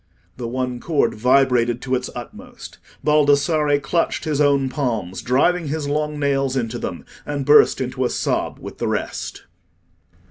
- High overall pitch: No, low, 135 Hz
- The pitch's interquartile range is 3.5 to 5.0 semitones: No, average, 2.9 semitones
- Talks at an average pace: Yes, average, 150 wpm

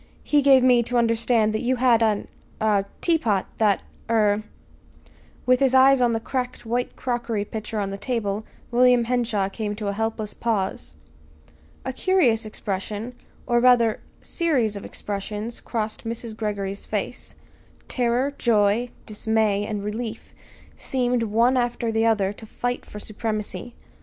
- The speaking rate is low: No, average, 145 wpm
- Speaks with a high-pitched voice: Yes, high, 225 Hz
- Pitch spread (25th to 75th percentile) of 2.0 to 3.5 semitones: Yes, average, 2.8 semitones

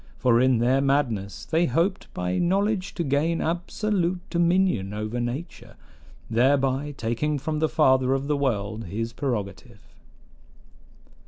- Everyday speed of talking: No, slow, 130 wpm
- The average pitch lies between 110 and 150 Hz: Yes, low, 135 Hz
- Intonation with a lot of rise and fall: Yes, wide, 6.3 semitones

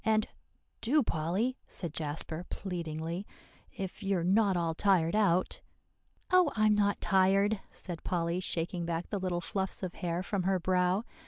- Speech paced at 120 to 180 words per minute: Yes, average, 155 wpm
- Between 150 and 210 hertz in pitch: Yes, medium, 185 Hz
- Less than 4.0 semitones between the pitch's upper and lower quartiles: Yes, average, 3.1 semitones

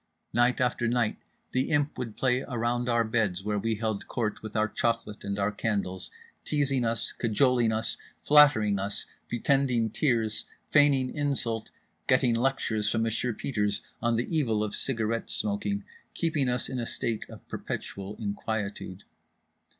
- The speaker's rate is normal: Yes, average, 150 wpm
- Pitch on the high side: No, low, 115 Hz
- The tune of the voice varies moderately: Yes, average, 3.0 semitones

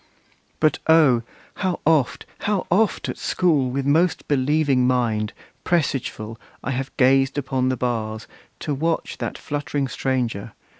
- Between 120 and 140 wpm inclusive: Yes, slow, 135 wpm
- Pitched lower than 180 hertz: Yes, low, 135 Hz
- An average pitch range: Yes, average, 3.8 semitones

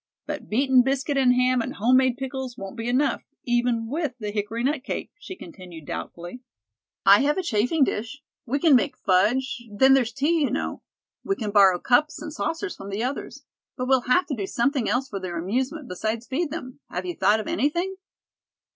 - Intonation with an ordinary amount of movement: Yes, average, 4.4 semitones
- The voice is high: Yes, very high, 255 Hz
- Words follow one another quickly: No, average, 195 wpm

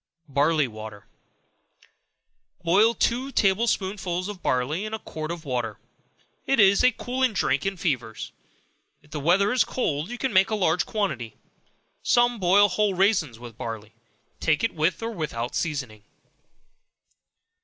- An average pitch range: No, wide, 7.2 semitones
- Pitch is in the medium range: Yes, medium, 175 Hz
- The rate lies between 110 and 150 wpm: Yes, average, 145 wpm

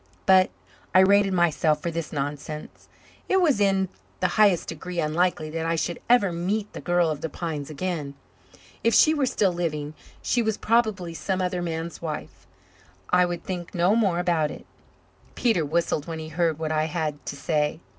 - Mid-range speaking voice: Yes, medium, 170 Hz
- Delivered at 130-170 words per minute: No, average, 180 wpm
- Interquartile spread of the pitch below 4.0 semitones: Yes, average, 3.3 semitones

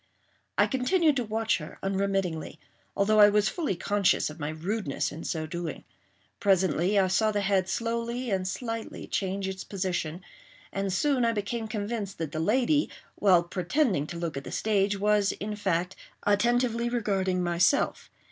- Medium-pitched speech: No, high, 200 Hz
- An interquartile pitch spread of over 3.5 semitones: Yes, average, 3.9 semitones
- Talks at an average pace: Yes, average, 160 wpm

